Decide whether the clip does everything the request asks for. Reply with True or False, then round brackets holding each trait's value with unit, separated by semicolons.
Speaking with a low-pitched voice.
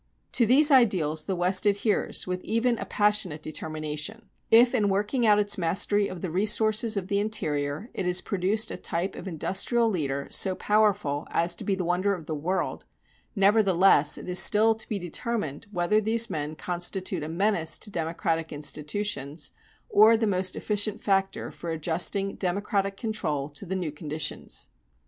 False (190 Hz)